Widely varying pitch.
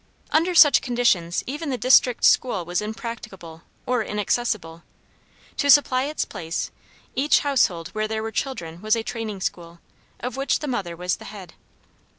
Yes: wide, 6.4 semitones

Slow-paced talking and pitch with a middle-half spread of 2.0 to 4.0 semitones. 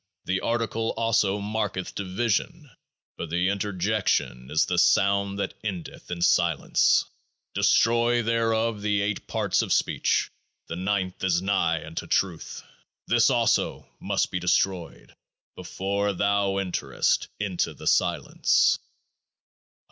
Yes: slow, 120 wpm; average, 2.8 semitones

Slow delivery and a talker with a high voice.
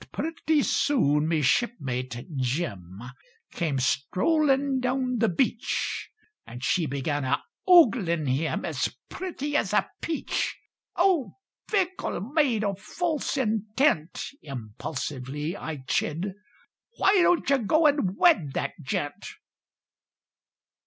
Yes: slow, 110 wpm; high, 200 Hz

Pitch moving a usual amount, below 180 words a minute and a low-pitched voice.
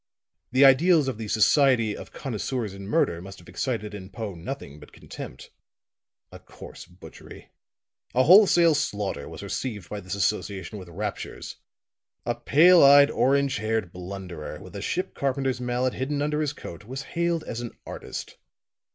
No: wide, 6.0 semitones; average, 160 wpm; low, 120 Hz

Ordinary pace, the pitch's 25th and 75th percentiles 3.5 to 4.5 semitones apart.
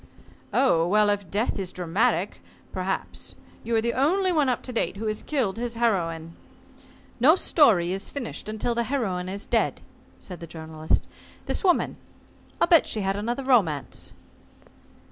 No: average, 160 wpm; average, 5.3 semitones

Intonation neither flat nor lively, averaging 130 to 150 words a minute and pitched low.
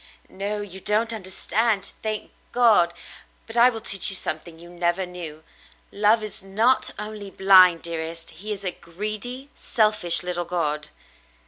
No: average, 3.7 semitones; average, 145 wpm; high, 195 Hz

